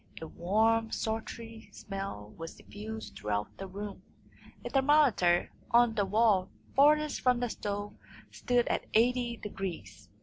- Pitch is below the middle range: No, high, 220 Hz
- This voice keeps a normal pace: No, slow, 130 wpm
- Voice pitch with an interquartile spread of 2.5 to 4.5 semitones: Yes, average, 4.1 semitones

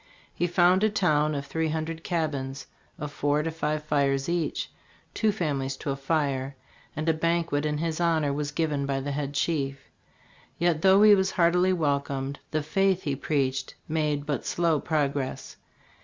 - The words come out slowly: No, average, 170 wpm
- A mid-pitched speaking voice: Yes, medium, 150 Hz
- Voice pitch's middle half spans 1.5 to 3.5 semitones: Yes, average, 3.0 semitones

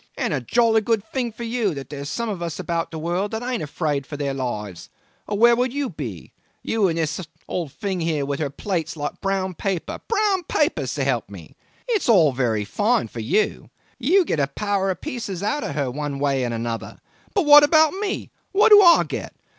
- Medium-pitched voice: Yes, medium, 180 Hz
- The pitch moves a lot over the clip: Yes, wide, 8.9 semitones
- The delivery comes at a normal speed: No, fast, 215 wpm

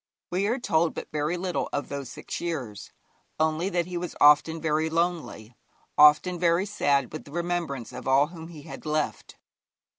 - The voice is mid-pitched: Yes, medium, 160 Hz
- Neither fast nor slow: Yes, average, 175 wpm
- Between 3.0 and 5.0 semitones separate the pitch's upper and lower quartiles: Yes, average, 3.3 semitones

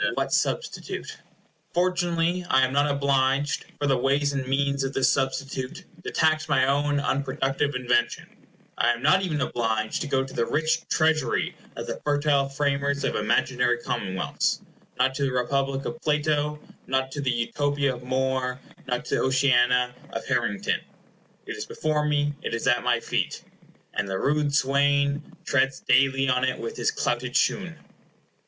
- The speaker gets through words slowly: No, average, 160 wpm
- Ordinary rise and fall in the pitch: No, narrow, 2.3 semitones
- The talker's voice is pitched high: No, low, 135 Hz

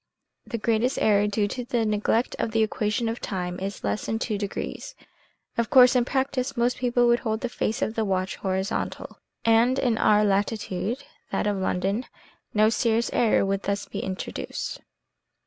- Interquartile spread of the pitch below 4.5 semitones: Yes, average, 2.9 semitones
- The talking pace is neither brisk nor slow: Yes, average, 175 wpm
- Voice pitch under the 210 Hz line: No, high, 220 Hz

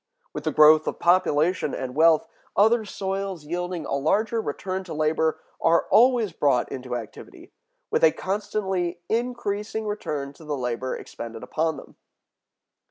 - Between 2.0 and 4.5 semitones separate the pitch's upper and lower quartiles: No, average, 5.2 semitones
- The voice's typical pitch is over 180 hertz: No, medium, 165 Hz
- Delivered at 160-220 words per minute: No, average, 145 wpm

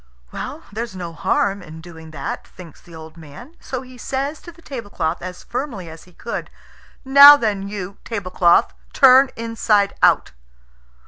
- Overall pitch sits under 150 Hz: No, high, 200 Hz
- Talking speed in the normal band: Yes, average, 150 wpm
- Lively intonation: Yes, wide, 6.9 semitones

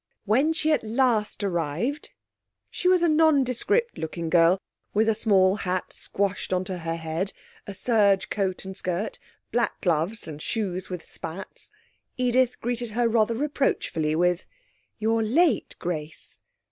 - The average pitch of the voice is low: No, high, 205 Hz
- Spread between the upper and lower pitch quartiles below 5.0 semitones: No, wide, 5.4 semitones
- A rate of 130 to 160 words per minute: Yes, average, 140 wpm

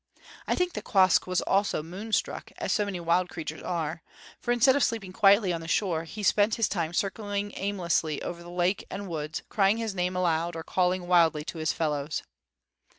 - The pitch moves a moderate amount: Yes, average, 3.4 semitones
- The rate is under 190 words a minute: No, average, 195 wpm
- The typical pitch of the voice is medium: Yes, medium, 180 Hz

